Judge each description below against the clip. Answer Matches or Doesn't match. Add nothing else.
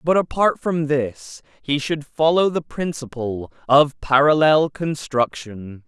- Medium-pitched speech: Matches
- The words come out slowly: Matches